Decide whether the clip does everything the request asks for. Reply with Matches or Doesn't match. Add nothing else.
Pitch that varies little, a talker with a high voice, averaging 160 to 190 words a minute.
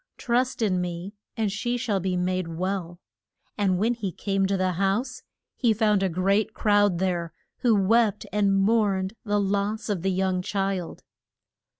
Matches